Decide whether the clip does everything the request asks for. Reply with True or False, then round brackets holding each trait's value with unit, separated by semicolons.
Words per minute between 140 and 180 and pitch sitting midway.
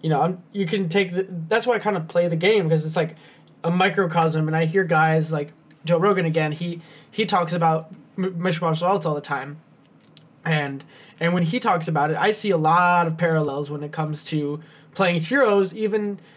False (205 wpm; 170 Hz)